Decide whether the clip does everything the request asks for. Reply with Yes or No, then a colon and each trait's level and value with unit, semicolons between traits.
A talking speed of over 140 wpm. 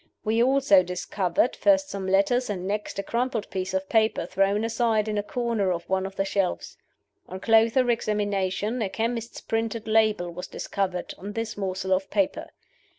Yes: average, 170 wpm